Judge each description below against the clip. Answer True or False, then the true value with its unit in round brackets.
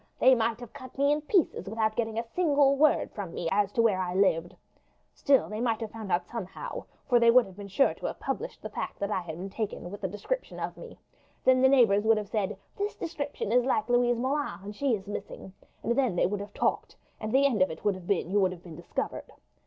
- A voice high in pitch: True (220 Hz)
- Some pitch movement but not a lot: True (4.8 semitones)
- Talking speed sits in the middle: False (250 wpm)